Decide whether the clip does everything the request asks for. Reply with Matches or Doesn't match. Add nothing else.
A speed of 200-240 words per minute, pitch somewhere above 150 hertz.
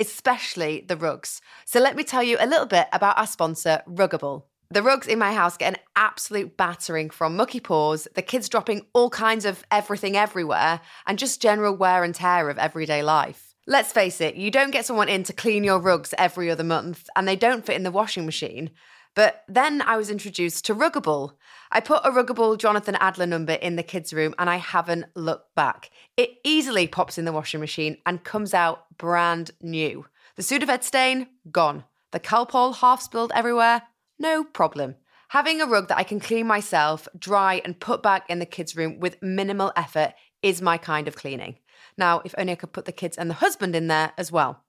Matches